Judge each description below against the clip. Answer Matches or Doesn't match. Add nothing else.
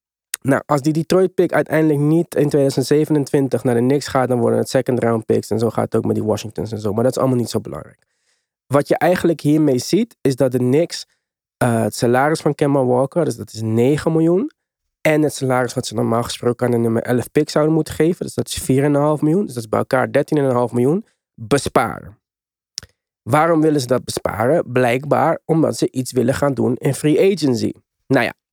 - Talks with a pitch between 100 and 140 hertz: Matches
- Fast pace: Matches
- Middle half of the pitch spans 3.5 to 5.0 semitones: Matches